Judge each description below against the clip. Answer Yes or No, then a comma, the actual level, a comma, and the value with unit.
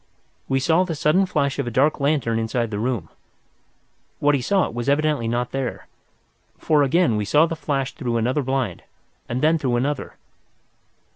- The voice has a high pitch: No, low, 135 Hz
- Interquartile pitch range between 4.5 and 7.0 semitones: No, average, 4.0 semitones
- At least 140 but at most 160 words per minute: No, average, 170 wpm